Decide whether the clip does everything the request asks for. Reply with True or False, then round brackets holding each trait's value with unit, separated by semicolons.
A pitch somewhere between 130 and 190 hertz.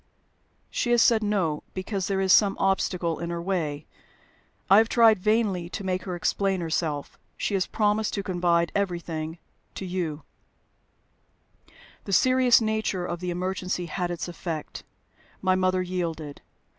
True (185 Hz)